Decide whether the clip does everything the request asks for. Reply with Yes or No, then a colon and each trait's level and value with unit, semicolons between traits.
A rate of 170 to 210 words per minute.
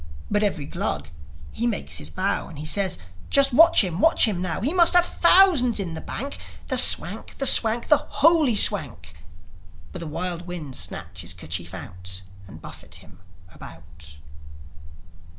No: average, 160 wpm